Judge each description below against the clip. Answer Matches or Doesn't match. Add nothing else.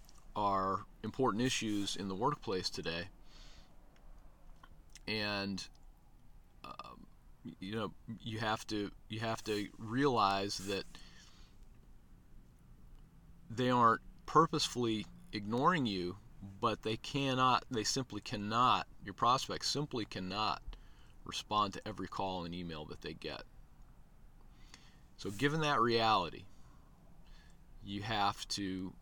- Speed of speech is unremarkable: Doesn't match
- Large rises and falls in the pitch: Doesn't match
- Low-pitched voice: Matches